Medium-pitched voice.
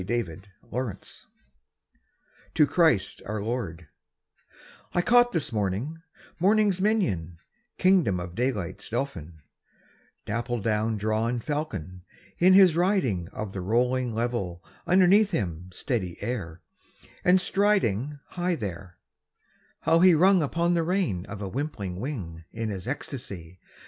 No: low, 120 Hz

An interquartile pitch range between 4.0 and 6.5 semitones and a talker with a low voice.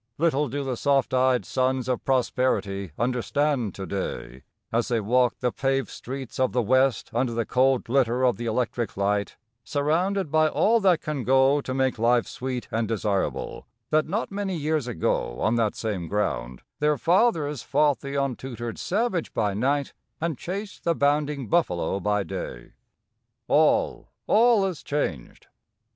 Yes: average, 4.4 semitones; low, 130 Hz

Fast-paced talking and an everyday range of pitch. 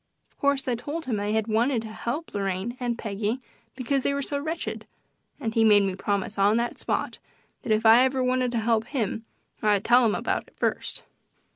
Yes: fast, 215 wpm; average, 3.2 semitones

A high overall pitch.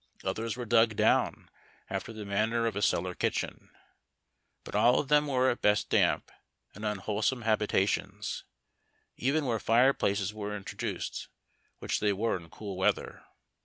No: low, 110 Hz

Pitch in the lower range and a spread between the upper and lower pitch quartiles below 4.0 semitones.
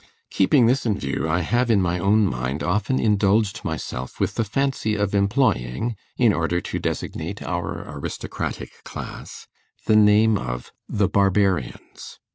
No: low, 100 Hz; average, 4.8 semitones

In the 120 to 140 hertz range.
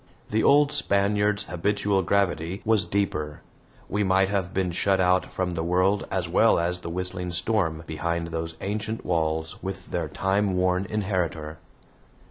No: very low, 95 Hz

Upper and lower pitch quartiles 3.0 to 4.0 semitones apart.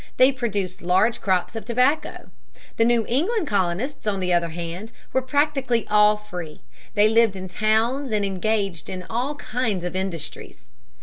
No: average, 5.2 semitones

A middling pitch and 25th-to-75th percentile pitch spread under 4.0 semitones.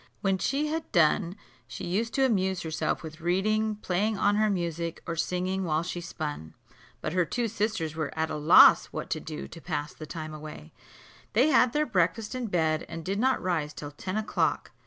No: medium, 180 Hz; average, 5.2 semitones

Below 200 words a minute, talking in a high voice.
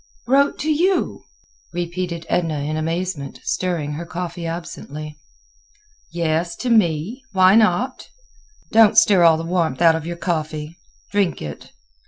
No: slow, 135 wpm; medium, 170 Hz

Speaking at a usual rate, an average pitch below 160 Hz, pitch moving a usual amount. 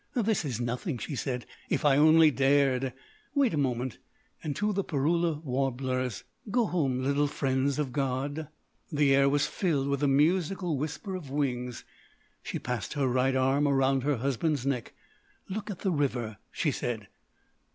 Yes: average, 160 wpm; medium, 140 Hz; average, 3.4 semitones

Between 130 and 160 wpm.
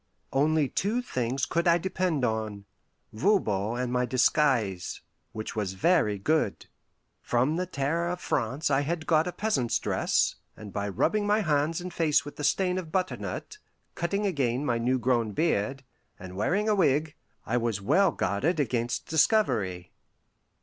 Yes: average, 155 wpm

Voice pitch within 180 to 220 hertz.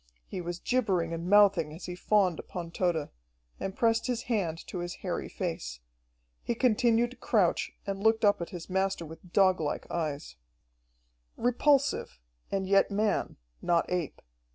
Yes: high, 190 Hz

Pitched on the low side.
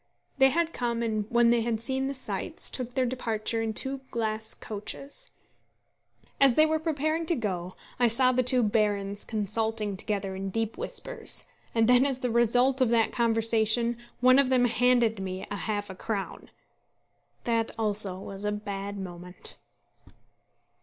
No: high, 230 Hz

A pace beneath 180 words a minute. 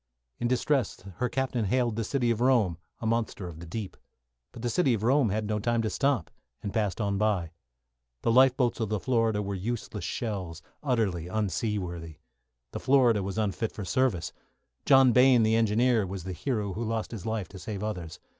No: average, 190 wpm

